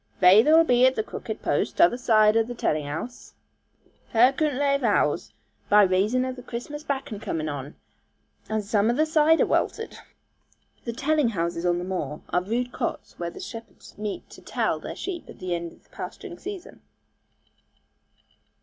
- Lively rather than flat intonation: Yes, wide, 7.1 semitones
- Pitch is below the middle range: No, high, 225 Hz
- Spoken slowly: No, average, 175 wpm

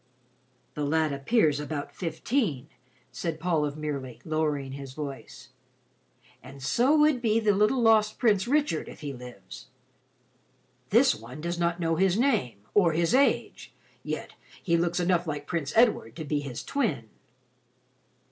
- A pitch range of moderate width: No, wide, 7.0 semitones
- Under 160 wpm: Yes, average, 145 wpm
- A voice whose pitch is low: No, medium, 160 Hz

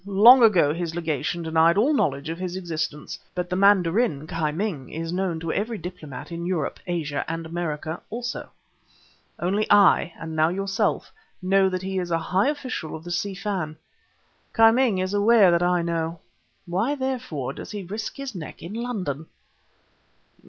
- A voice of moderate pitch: Yes, medium, 180 Hz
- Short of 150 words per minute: No, average, 170 wpm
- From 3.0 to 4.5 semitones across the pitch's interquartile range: Yes, average, 3.9 semitones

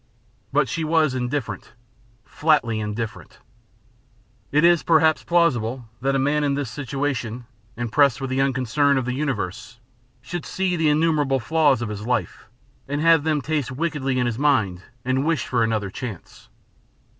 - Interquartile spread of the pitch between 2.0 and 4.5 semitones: Yes, average, 4.0 semitones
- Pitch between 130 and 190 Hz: Yes, low, 135 Hz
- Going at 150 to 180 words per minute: Yes, average, 155 wpm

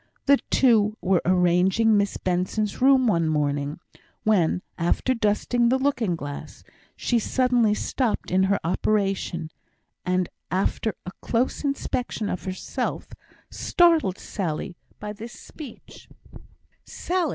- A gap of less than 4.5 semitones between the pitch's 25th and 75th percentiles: No, average, 5.2 semitones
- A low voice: No, high, 205 Hz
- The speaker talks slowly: Yes, slow, 120 wpm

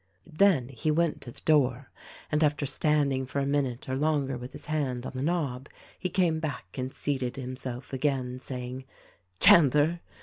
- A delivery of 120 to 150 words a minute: No, average, 170 wpm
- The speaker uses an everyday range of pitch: Yes, average, 3.0 semitones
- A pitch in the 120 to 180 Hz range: Yes, low, 135 Hz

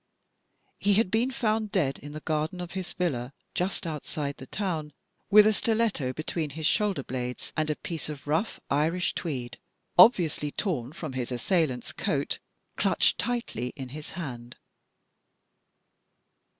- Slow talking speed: No, average, 145 wpm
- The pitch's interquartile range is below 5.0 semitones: No, wide, 5.6 semitones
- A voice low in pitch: No, medium, 155 Hz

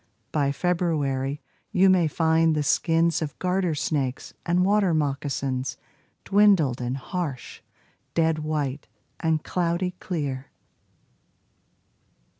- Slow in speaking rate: Yes, slow, 100 wpm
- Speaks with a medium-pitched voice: Yes, medium, 160 Hz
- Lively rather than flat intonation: No, average, 4.0 semitones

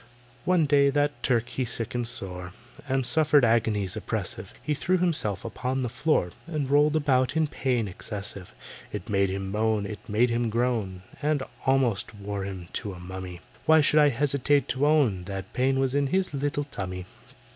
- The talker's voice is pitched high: No, low, 125 Hz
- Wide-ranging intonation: Yes, wide, 6.4 semitones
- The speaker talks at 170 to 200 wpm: Yes, average, 175 wpm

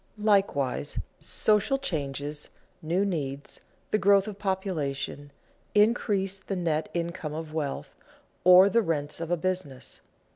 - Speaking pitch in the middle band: Yes, medium, 175 Hz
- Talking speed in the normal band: No, slow, 120 wpm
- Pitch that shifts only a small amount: No, average, 4.9 semitones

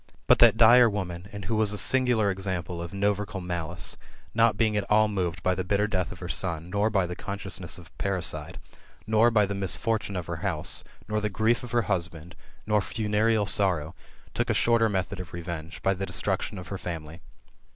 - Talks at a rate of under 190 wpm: No, fast, 205 wpm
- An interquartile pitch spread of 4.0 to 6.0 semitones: No, average, 3.3 semitones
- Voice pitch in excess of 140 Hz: No, very low, 95 Hz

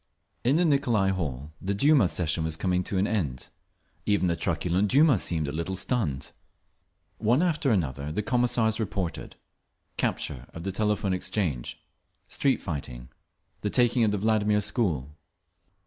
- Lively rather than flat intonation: Yes, wide, 5.7 semitones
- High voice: No, very low, 95 Hz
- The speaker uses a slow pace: No, average, 145 wpm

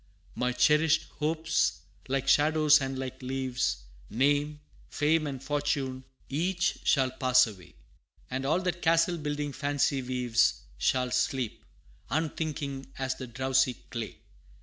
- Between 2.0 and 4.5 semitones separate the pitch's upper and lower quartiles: Yes, average, 2.9 semitones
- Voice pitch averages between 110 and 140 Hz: Yes, low, 135 Hz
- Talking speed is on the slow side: Yes, slow, 125 wpm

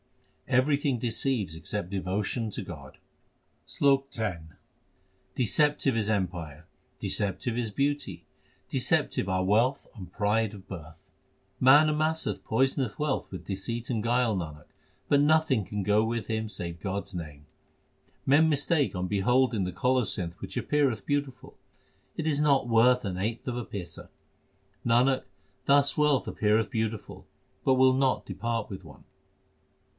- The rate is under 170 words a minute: Yes, average, 140 wpm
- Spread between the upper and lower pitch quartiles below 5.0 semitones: No, wide, 5.5 semitones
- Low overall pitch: Yes, low, 115 Hz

